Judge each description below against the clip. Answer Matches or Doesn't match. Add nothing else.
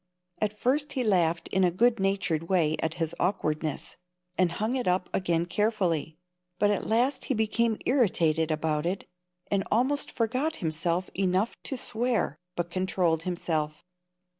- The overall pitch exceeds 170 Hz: Matches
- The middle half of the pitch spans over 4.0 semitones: Matches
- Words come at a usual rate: Matches